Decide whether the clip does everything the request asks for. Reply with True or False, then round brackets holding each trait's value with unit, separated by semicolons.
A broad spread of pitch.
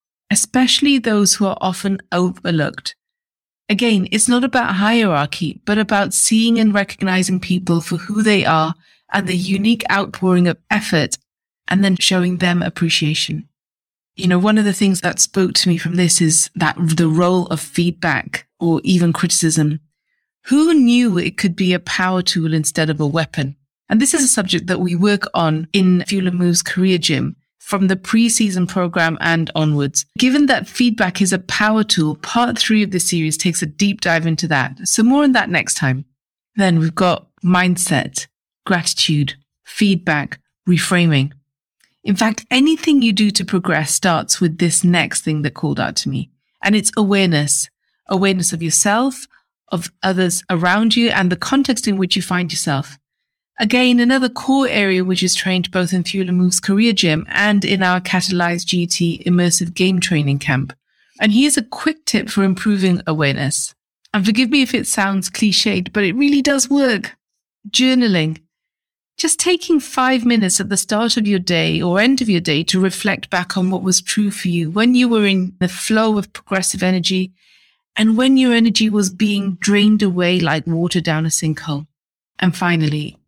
False (4.0 semitones)